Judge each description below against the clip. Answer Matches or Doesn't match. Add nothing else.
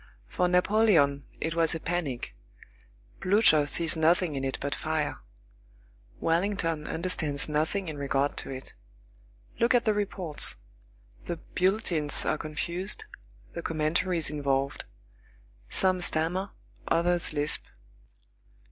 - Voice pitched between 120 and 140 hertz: Doesn't match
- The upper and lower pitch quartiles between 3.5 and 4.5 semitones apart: Matches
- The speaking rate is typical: Doesn't match